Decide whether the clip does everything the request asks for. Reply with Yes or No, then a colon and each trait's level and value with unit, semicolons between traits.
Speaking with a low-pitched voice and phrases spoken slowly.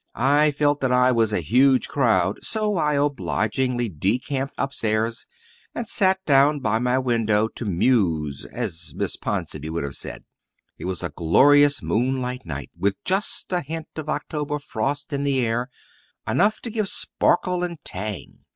No: low, 125 Hz; average, 160 wpm